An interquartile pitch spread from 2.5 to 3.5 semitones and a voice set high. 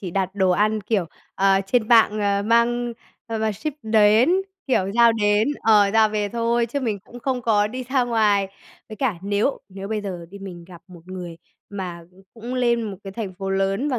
Yes: average, 3.1 semitones; high, 210 Hz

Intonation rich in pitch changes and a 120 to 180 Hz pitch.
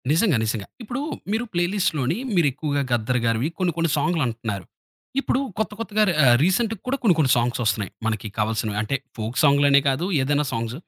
Yes: wide, 7.3 semitones; medium, 140 Hz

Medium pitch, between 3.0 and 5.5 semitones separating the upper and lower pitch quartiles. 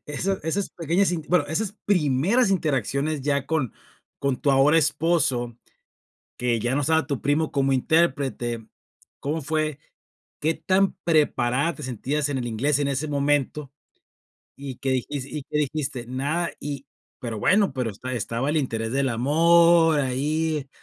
Yes: medium, 145 Hz; average, 3.5 semitones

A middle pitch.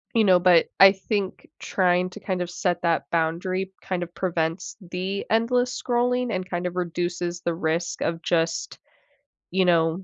Yes: medium, 180 Hz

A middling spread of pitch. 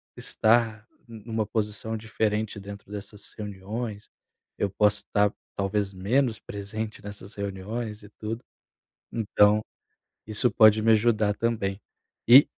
No: narrow, 1.5 semitones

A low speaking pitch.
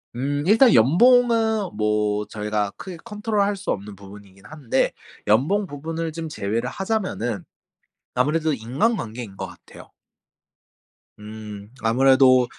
Yes: low, 130 Hz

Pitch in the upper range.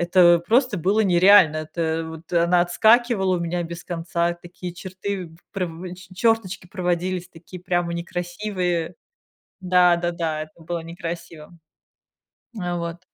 No: medium, 175 Hz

